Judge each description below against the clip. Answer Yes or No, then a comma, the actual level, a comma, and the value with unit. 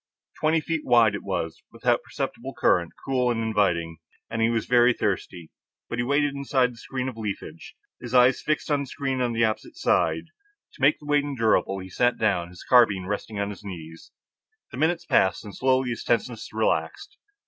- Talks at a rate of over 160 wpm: Yes, average, 190 wpm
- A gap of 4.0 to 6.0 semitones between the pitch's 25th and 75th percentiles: Yes, average, 4.7 semitones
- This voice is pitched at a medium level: No, low, 120 Hz